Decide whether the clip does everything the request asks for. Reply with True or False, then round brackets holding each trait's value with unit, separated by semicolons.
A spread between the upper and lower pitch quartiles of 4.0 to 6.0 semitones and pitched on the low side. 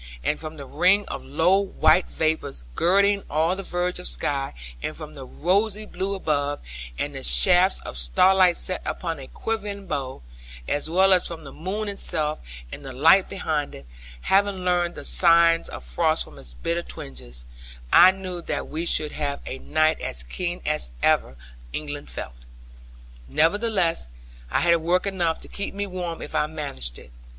False (4.4 semitones; 165 Hz)